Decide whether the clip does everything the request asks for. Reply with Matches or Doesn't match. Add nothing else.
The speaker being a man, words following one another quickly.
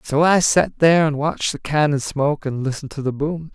Matches